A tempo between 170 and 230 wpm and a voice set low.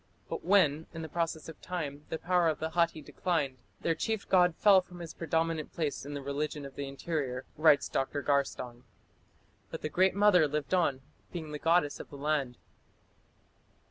No: average, 180 wpm; medium, 155 Hz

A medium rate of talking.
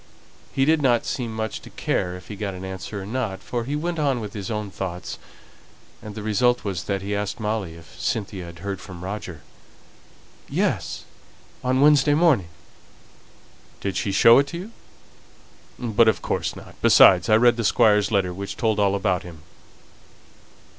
Yes: average, 175 wpm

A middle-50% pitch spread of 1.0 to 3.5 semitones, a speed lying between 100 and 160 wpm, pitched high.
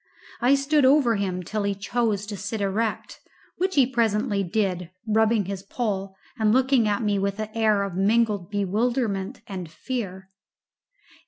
Yes: average, 3.1 semitones; average, 155 wpm; high, 210 Hz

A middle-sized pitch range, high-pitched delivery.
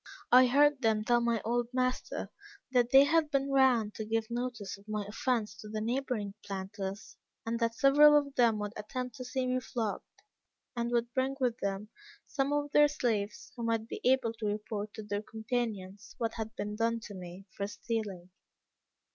Yes: average, 3.3 semitones; high, 230 Hz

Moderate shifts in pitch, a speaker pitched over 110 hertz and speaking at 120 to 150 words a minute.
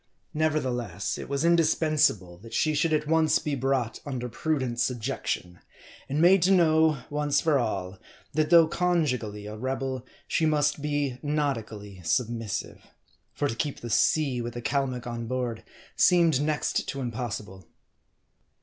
Yes: average, 4.8 semitones; low, 135 Hz; average, 145 wpm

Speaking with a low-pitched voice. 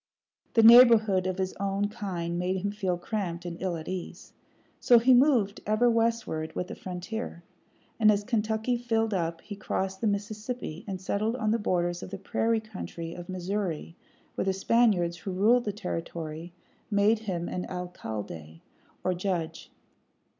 No: high, 195 Hz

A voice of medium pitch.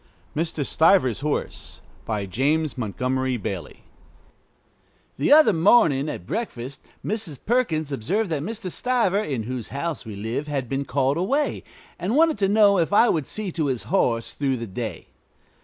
Yes: medium, 150 Hz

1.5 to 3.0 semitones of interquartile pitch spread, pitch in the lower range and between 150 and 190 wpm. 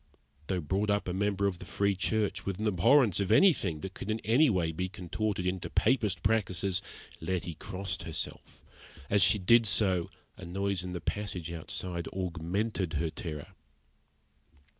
Yes: average, 2.7 semitones; very low, 95 Hz; average, 160 wpm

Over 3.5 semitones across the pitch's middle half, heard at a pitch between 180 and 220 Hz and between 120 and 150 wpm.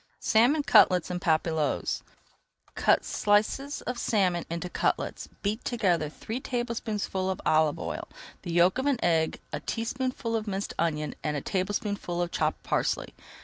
Yes: average, 5.2 semitones; high, 190 Hz; average, 145 wpm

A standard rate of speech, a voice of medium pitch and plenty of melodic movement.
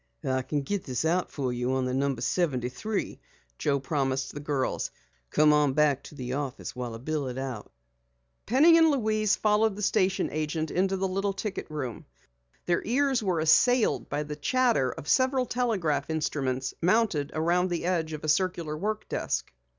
Yes: average, 175 wpm; medium, 155 Hz; wide, 6.7 semitones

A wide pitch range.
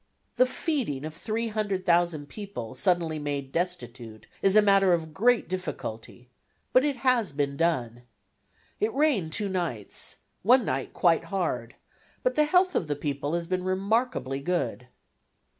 Yes: wide, 6.9 semitones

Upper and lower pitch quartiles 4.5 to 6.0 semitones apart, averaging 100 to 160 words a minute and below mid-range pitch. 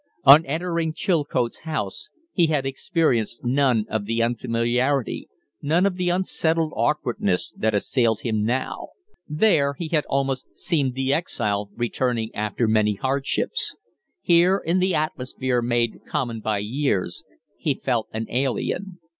Yes: wide, 5.5 semitones; slow, 135 wpm; low, 130 Hz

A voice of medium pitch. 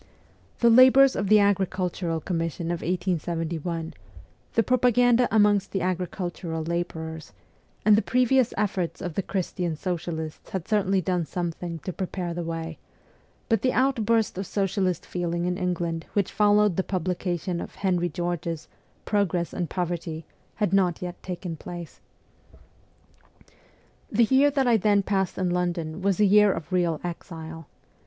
Yes: medium, 180 Hz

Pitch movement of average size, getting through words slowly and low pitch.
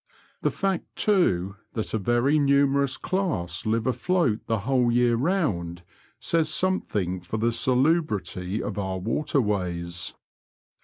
No: wide, 7.3 semitones; slow, 120 wpm; low, 115 Hz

